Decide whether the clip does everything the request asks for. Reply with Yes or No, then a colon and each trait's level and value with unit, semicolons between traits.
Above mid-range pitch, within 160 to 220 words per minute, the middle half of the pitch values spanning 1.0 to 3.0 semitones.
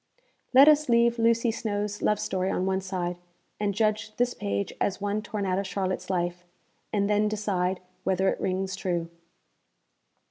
Yes: high, 200 Hz; average, 165 wpm; narrow, 2.5 semitones